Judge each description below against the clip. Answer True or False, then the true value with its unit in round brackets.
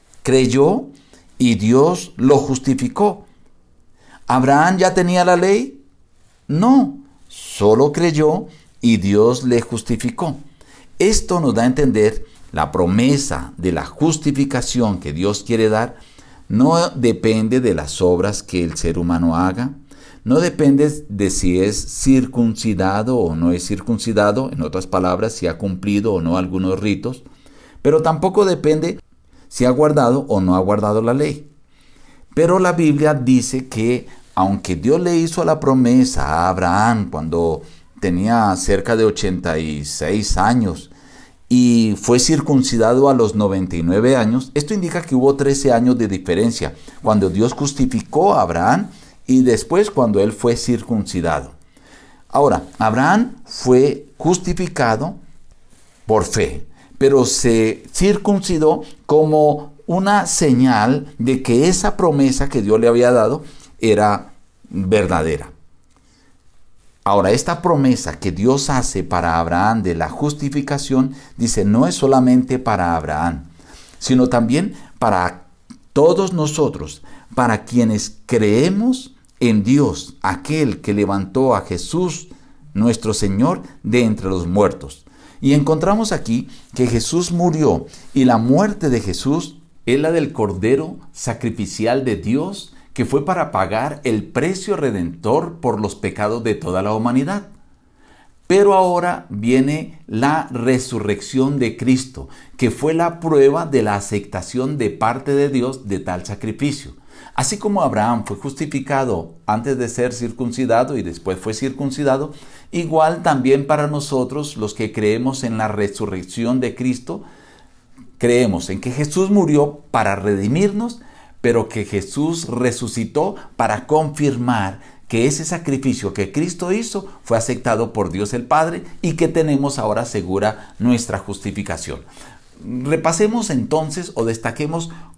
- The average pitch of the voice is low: True (125 Hz)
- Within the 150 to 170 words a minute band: False (130 wpm)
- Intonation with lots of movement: True (5.9 semitones)